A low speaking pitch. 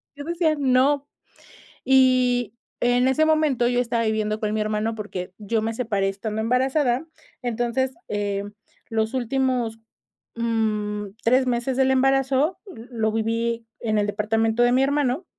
No: high, 240 Hz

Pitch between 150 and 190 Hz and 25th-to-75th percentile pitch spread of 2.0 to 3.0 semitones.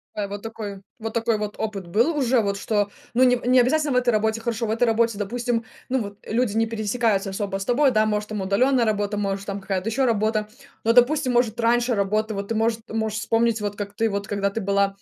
No: high, 220 Hz; average, 2.7 semitones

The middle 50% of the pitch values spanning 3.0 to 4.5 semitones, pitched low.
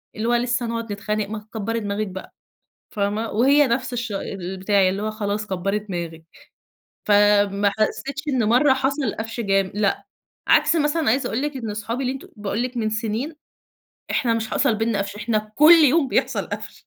No: average, 3.5 semitones; high, 220 Hz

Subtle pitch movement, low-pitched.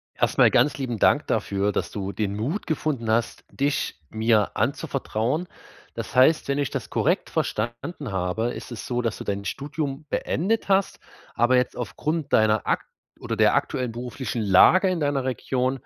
No: average, 4.7 semitones; low, 125 Hz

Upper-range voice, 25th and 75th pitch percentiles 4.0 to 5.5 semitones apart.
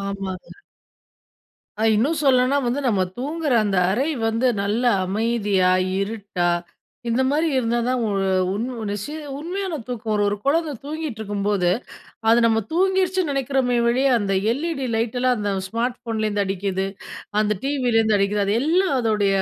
Yes: high, 230 Hz; average, 5.2 semitones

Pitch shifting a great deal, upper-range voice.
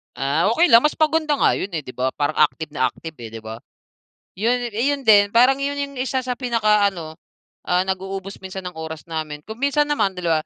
Yes: wide, 8.0 semitones; high, 195 Hz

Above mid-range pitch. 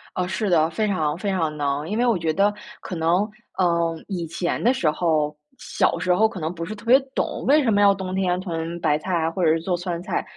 No: medium, 175 Hz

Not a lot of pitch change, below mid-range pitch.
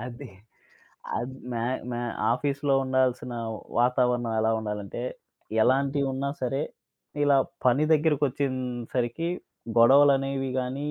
Yes: narrow, 2.3 semitones; low, 130 Hz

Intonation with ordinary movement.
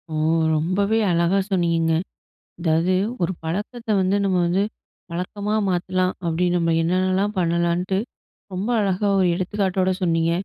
No: narrow, 2.3 semitones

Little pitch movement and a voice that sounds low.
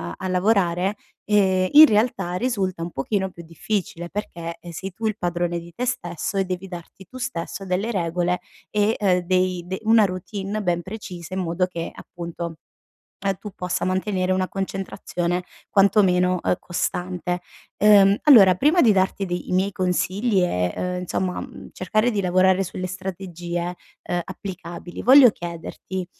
No: narrow, 2.1 semitones; medium, 185 Hz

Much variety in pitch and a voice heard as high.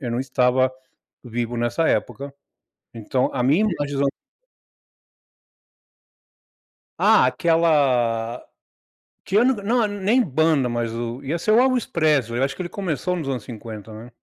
No: wide, 6.1 semitones; low, 135 Hz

